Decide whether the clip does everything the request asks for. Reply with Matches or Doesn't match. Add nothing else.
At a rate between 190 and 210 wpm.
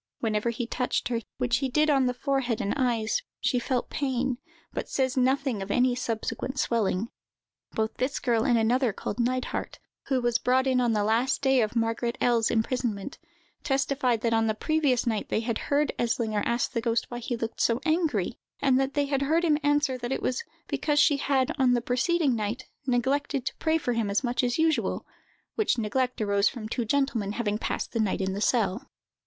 Matches